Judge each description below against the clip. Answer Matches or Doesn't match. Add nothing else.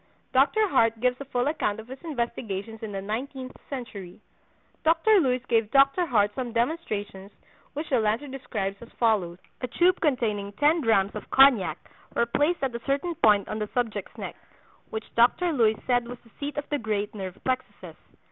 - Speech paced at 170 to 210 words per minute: Matches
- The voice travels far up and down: Doesn't match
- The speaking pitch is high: Matches